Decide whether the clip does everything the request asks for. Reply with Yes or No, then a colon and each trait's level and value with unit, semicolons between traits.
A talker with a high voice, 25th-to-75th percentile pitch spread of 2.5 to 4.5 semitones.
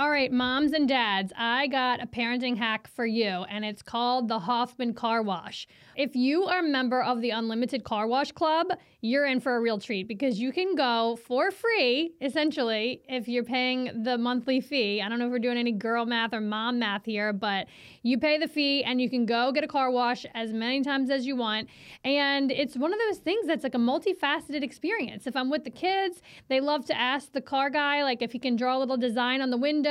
Yes: very high, 255 Hz; average, 3.3 semitones